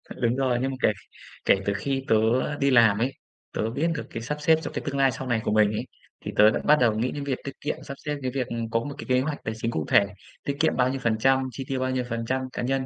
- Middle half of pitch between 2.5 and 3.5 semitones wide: Yes, average, 3.0 semitones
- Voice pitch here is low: Yes, low, 130 Hz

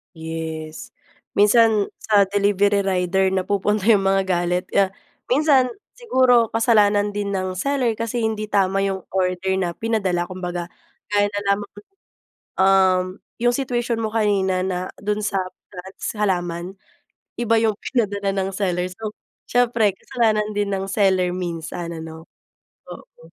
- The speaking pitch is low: No, high, 200 Hz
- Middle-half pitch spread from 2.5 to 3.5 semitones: Yes, average, 2.8 semitones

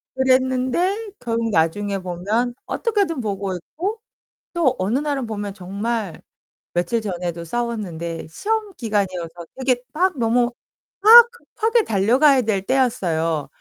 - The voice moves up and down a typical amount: No, wide, 6.6 semitones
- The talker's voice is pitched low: No, high, 230 Hz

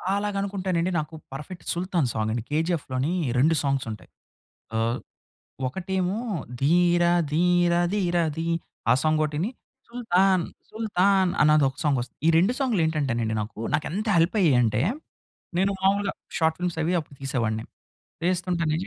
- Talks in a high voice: No, medium, 170 Hz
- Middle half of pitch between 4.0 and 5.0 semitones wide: Yes, average, 4.7 semitones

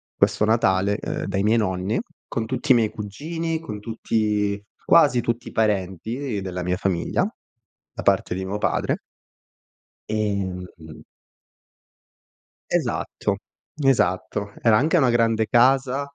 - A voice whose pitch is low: Yes, low, 110 Hz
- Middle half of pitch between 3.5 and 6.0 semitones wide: Yes, average, 4.0 semitones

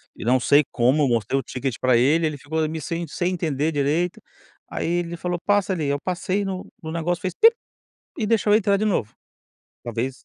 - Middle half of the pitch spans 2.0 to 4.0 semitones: No, average, 4.9 semitones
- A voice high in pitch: No, medium, 160 Hz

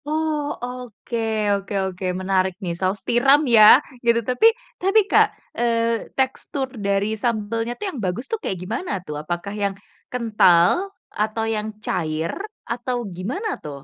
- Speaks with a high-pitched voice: Yes, high, 225 Hz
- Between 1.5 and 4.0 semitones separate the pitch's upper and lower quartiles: No, average, 4.9 semitones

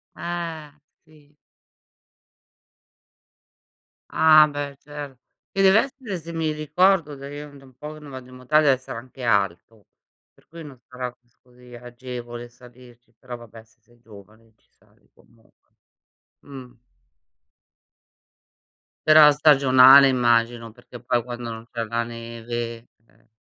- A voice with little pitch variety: No, average, 3.9 semitones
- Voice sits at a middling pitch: No, low, 125 Hz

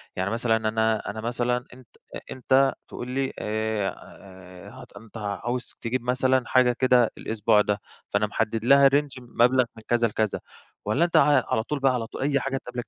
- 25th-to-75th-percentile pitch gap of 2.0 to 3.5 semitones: Yes, average, 2.9 semitones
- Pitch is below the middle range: Yes, low, 120 Hz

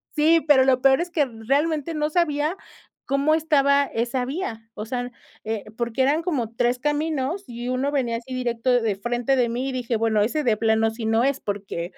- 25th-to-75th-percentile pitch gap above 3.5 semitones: Yes, average, 4.1 semitones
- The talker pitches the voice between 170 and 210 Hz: No, very high, 255 Hz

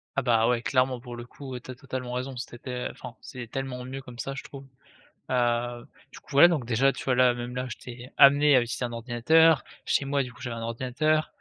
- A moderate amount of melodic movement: No, narrow, 2.1 semitones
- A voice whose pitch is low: Yes, low, 125 Hz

